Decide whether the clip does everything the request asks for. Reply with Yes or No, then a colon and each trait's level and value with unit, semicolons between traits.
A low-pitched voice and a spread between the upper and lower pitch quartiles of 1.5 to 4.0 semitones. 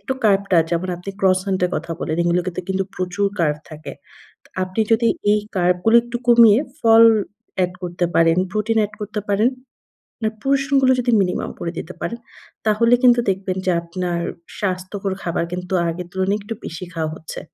No: high, 190 Hz; average, 3.7 semitones